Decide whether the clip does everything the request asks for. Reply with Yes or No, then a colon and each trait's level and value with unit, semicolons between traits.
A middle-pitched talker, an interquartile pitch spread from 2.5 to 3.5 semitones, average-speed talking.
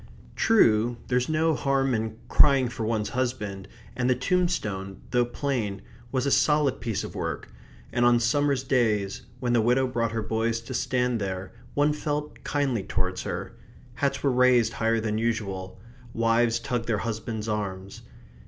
No: low, 120 Hz; average, 3.2 semitones; average, 160 wpm